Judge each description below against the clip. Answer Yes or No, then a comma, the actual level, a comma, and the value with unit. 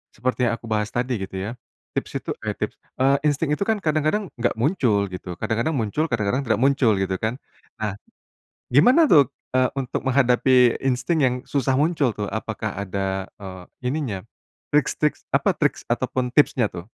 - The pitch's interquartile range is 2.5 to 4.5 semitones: No, average, 4.9 semitones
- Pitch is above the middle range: No, low, 125 Hz